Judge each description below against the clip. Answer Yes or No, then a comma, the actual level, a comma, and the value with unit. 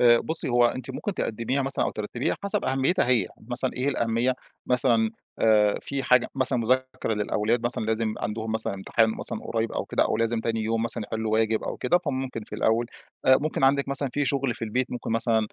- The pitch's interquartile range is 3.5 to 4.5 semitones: No, average, 2.8 semitones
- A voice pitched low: Yes, low, 120 Hz